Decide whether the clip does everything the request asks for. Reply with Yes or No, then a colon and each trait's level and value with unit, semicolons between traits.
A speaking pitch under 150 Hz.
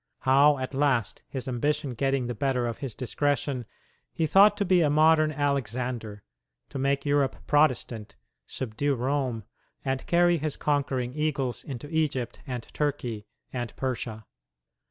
Yes: low, 135 Hz